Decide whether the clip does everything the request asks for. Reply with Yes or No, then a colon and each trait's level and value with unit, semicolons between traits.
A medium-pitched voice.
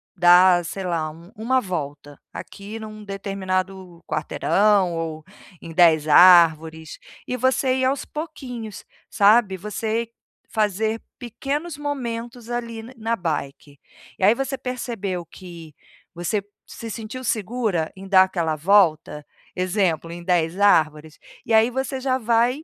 No: high, 195 Hz